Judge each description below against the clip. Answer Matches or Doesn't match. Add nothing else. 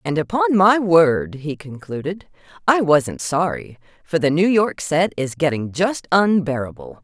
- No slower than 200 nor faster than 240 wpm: Doesn't match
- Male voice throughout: Doesn't match